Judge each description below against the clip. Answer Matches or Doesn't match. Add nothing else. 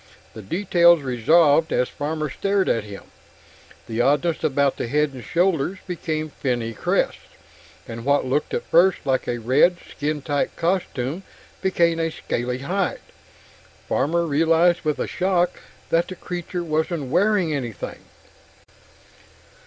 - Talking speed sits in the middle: Doesn't match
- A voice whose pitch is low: Doesn't match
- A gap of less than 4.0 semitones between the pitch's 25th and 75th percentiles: Doesn't match